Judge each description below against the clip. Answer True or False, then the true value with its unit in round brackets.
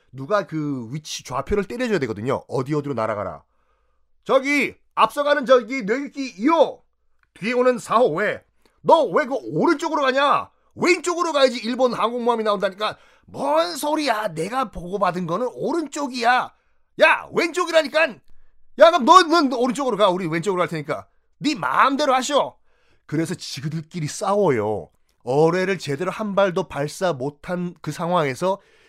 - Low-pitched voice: False (230 Hz)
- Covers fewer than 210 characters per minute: False (320 characters per minute)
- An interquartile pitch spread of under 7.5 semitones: False (8.8 semitones)